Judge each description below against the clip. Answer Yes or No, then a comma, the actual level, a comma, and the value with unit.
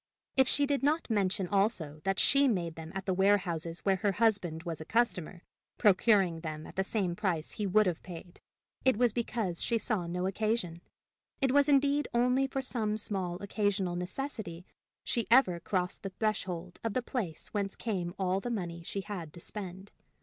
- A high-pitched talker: Yes, high, 195 Hz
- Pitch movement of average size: Yes, average, 4.5 semitones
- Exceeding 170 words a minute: Yes, average, 185 wpm